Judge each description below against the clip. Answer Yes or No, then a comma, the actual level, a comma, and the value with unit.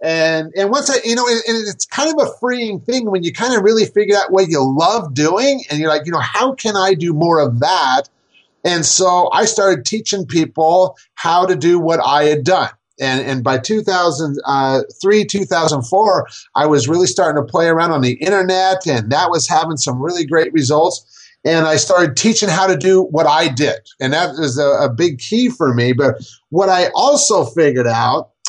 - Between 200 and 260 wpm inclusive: Yes, fast, 205 wpm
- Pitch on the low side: No, medium, 170 Hz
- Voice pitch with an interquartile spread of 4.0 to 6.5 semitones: Yes, average, 4.8 semitones